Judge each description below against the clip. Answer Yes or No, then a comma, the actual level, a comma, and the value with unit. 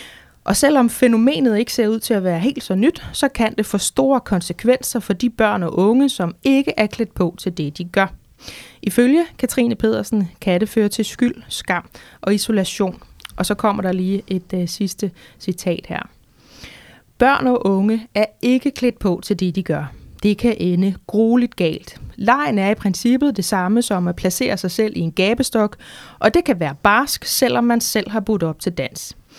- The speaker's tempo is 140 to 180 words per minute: No, average, 195 wpm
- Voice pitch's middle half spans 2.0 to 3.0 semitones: No, average, 4.4 semitones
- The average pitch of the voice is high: Yes, high, 215 Hz